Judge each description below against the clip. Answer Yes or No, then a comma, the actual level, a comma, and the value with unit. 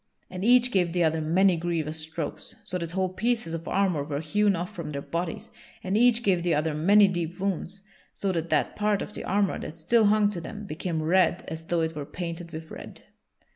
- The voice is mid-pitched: Yes, medium, 175 Hz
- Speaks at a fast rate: Yes, fast, 215 wpm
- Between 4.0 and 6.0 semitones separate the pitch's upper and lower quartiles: No, average, 3.6 semitones